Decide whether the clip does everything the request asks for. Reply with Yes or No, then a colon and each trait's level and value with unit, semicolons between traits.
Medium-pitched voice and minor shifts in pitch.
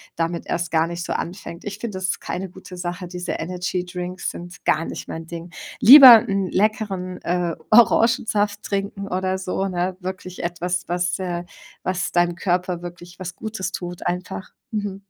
Yes: medium, 180 Hz; narrow, 1.9 semitones